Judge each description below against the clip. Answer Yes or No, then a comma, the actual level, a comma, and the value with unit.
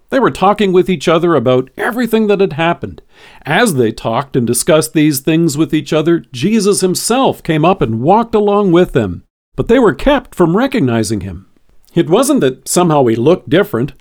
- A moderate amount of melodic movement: No, wide, 6.9 semitones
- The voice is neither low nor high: Yes, medium, 165 Hz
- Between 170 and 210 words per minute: Yes, average, 190 wpm